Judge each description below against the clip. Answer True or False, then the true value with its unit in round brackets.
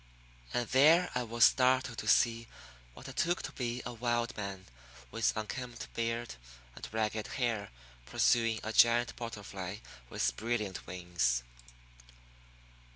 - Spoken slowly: True (130 wpm)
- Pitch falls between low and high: False (115 Hz)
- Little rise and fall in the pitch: True (2.3 semitones)